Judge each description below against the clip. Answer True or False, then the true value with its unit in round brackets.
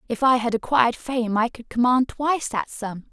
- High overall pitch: True (240 Hz)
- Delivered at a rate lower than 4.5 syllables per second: False (5.1 syllables/s)